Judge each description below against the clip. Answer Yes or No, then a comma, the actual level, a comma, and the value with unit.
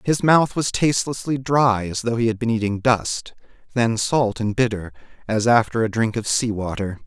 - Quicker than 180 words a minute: Yes, average, 195 wpm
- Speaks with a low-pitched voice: Yes, low, 115 Hz